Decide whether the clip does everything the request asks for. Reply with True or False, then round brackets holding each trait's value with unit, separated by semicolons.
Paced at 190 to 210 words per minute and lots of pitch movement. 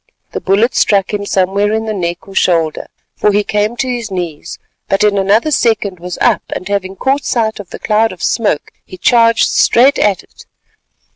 False (195 wpm; 3.0 semitones)